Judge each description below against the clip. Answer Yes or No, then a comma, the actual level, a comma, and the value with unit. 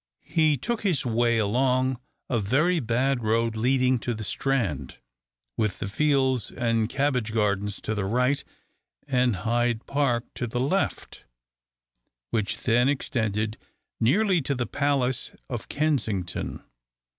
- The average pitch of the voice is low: Yes, low, 120 Hz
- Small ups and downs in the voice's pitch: No, average, 3.6 semitones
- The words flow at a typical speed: No, slow, 130 wpm